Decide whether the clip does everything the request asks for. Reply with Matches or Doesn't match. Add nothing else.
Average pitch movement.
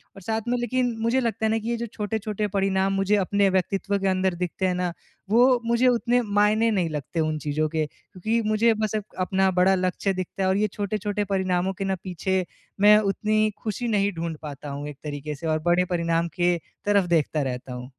Matches